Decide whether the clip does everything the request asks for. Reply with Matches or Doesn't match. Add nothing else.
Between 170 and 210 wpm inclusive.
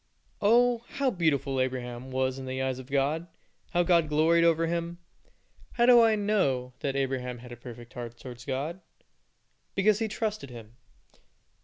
Doesn't match